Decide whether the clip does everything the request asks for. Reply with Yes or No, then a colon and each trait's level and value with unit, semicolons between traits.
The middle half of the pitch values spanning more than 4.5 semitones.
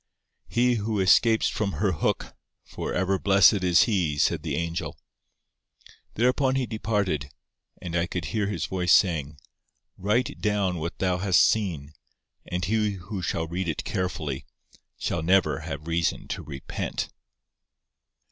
No: average, 3.9 semitones